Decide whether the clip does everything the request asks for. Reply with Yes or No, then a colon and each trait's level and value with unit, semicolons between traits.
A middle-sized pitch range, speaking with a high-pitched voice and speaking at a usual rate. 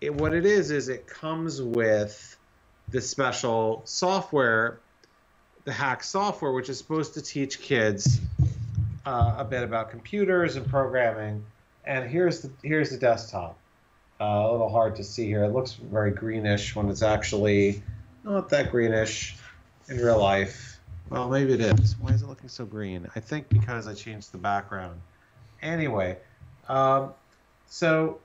No: average, 4.4 semitones; low, 115 Hz; average, 155 wpm